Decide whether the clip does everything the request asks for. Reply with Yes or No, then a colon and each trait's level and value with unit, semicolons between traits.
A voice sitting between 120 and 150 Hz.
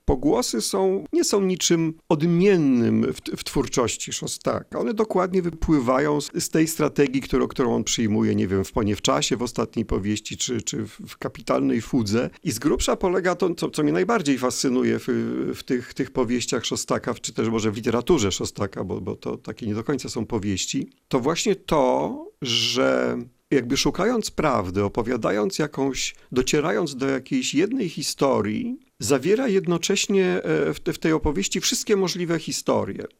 Yes: medium, 140 Hz